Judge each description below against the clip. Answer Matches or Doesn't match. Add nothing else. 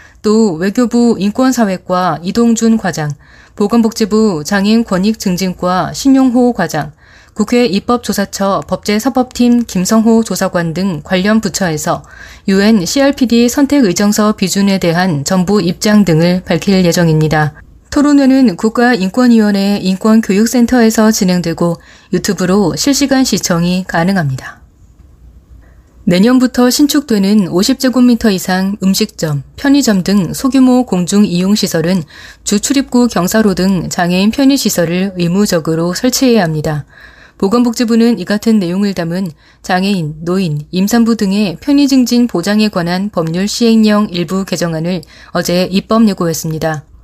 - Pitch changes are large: Doesn't match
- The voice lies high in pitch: Matches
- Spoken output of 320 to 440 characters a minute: Doesn't match